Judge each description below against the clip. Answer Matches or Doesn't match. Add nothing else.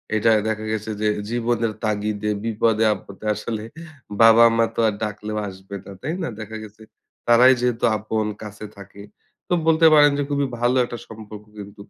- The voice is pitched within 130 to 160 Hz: Doesn't match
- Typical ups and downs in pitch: Doesn't match